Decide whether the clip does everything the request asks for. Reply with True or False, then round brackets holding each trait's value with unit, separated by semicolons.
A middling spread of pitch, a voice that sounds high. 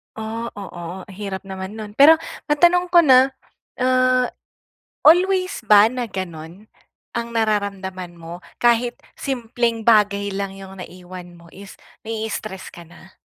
True (4.5 semitones; 210 Hz)